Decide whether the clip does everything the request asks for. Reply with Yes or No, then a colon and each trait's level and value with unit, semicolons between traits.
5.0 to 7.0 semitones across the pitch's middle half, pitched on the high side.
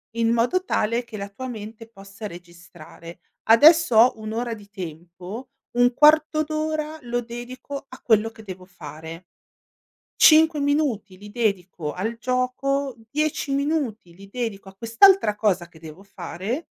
Yes: wide, 5.5 semitones; high, 225 Hz